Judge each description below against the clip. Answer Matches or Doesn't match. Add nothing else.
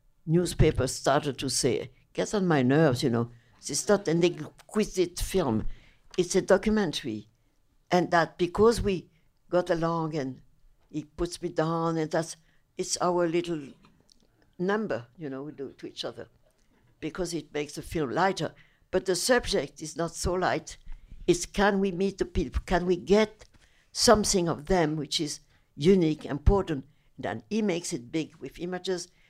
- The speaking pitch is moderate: Matches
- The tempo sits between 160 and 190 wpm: Matches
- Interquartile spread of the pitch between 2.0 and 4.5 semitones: Matches